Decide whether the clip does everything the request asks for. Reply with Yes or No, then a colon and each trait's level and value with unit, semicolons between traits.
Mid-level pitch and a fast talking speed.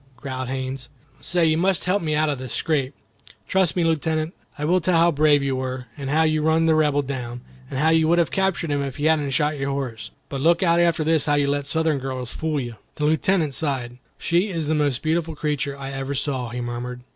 Yes: medium, 150 Hz; fast, 235 wpm